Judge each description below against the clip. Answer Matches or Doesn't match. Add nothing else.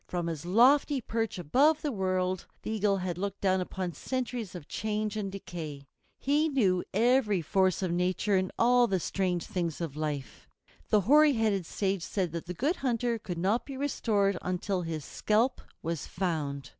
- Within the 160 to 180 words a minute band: Matches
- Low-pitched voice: Doesn't match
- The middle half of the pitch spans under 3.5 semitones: Doesn't match